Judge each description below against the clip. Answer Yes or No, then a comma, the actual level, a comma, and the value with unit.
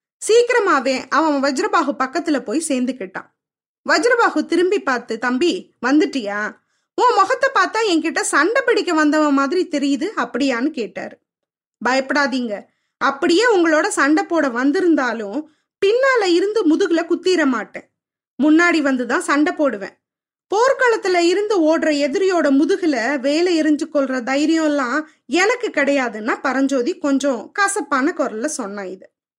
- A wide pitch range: No, average, 4.8 semitones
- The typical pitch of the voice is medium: No, very high, 305 Hz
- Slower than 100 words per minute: No, average, 110 wpm